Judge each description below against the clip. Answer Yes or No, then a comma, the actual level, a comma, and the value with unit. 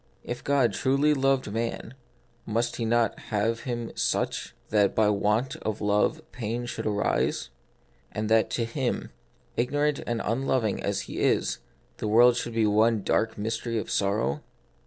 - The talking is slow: No, average, 165 wpm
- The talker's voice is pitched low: Yes, low, 115 Hz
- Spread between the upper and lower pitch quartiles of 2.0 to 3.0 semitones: Yes, narrow, 2.4 semitones